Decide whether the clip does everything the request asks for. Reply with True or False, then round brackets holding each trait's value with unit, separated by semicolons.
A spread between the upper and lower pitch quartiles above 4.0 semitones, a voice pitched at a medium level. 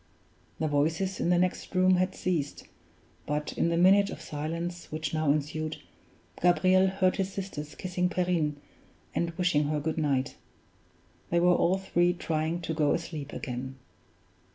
False (3.3 semitones; 170 Hz)